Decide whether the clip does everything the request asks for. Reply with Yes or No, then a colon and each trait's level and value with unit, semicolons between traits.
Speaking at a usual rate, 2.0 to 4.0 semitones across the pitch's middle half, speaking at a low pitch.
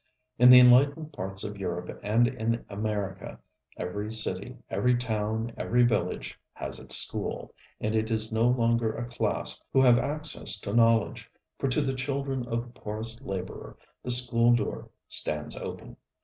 Yes: average, 160 wpm; narrow, 2.6 semitones; low, 115 Hz